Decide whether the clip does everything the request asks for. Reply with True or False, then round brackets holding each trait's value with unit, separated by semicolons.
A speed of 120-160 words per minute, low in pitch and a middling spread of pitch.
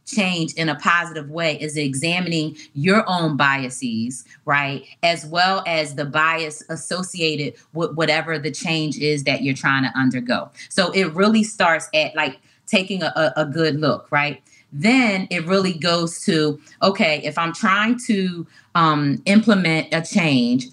False (155 wpm; 160 Hz; 3.9 semitones)